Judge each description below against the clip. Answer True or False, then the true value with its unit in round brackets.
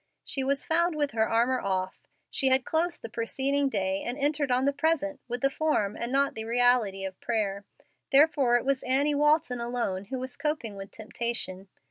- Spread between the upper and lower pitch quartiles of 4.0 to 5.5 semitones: True (4.3 semitones)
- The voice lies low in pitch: False (250 Hz)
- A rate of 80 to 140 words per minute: False (190 wpm)